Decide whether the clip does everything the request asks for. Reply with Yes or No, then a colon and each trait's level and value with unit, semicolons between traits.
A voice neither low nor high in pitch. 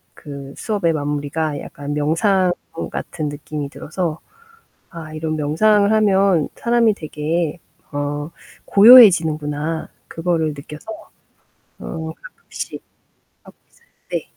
Yes: medium, 160 Hz